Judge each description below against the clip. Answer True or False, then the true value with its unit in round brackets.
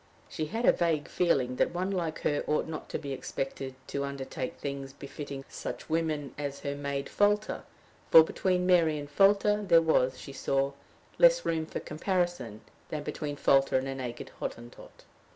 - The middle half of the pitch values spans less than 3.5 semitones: False (4.1 semitones)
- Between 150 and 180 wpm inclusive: True (170 wpm)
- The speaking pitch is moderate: True (145 Hz)